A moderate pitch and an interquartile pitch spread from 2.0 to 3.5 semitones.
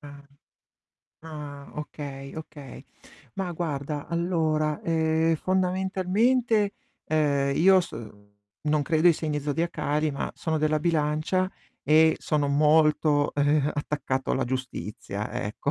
Yes: medium, 155 Hz; narrow, 2.6 semitones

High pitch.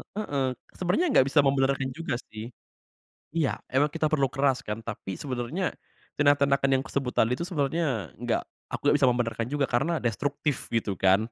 No: low, 135 Hz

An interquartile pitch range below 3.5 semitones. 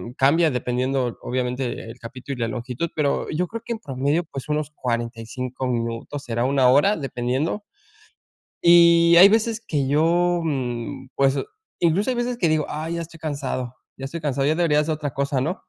No: average, 4.8 semitones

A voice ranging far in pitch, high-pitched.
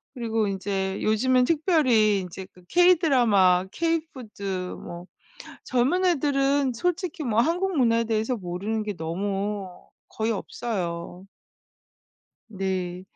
Yes: wide, 6.1 semitones; high, 220 Hz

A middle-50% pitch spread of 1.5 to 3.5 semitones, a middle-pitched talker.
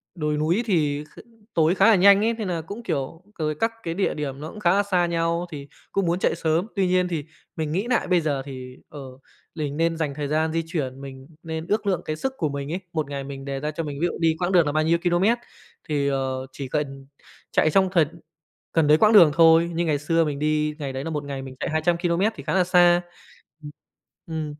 Yes: average, 3.2 semitones; medium, 160 Hz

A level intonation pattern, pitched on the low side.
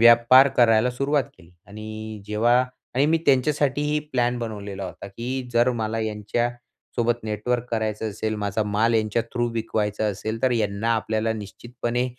Yes: narrow, 2.2 semitones; low, 115 Hz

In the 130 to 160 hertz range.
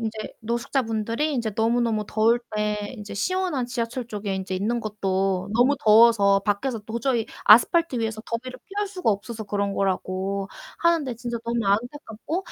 No: high, 225 Hz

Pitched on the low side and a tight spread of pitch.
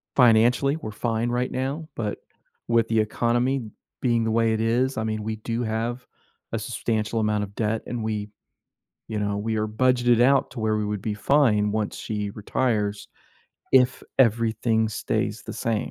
Yes: low, 115 Hz; narrow, 2.1 semitones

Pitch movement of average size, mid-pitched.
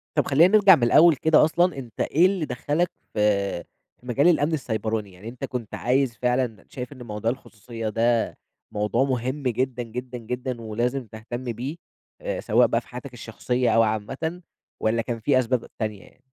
No: average, 3.5 semitones; low, 125 Hz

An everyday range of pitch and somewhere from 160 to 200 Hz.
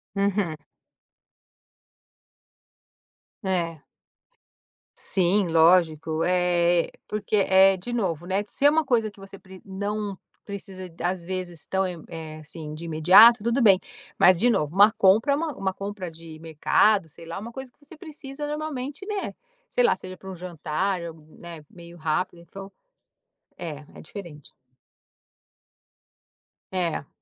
Yes: average, 3.9 semitones; medium, 185 Hz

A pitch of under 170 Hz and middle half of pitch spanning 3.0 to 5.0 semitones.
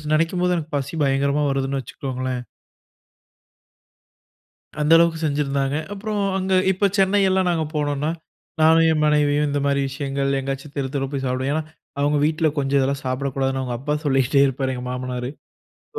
No: medium, 140 Hz; narrow, 2.6 semitones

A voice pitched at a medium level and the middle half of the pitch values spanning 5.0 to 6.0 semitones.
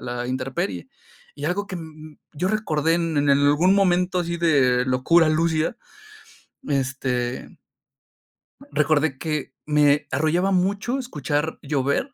No: medium, 155 Hz; average, 3.9 semitones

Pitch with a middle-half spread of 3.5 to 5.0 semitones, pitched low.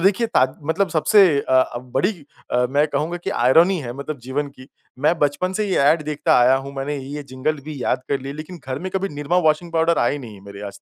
No: average, 4.2 semitones; medium, 145 Hz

